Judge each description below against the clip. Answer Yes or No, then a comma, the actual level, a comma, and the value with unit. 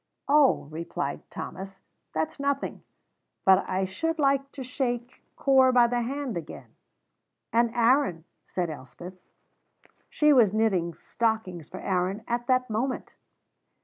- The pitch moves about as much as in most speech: No, wide, 6.1 semitones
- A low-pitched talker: No, high, 230 Hz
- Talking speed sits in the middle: No, slow, 125 wpm